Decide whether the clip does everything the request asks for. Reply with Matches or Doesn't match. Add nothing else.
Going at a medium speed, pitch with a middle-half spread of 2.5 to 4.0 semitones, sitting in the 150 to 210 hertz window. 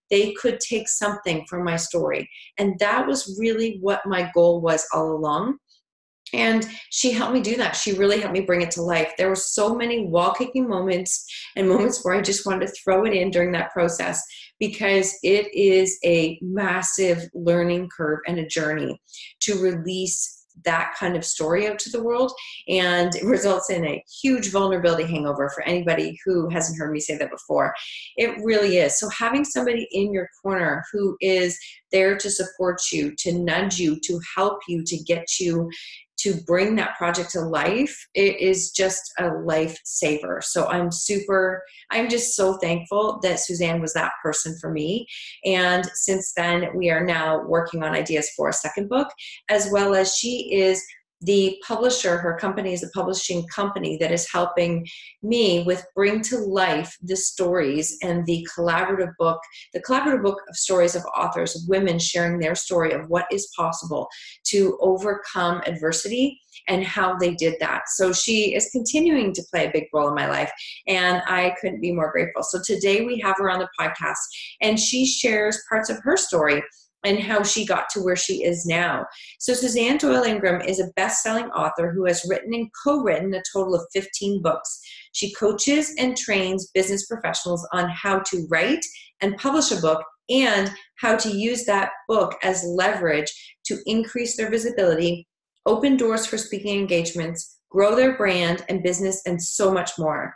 Matches